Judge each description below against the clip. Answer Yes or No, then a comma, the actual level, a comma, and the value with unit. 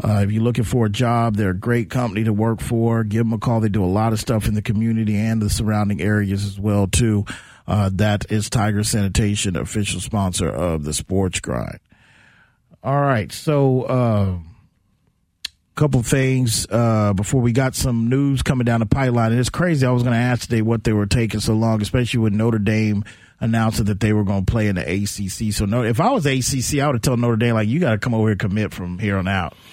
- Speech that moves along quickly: Yes, fast, 235 wpm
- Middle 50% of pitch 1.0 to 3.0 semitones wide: Yes, narrow, 2.6 semitones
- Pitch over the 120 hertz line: No, low, 110 Hz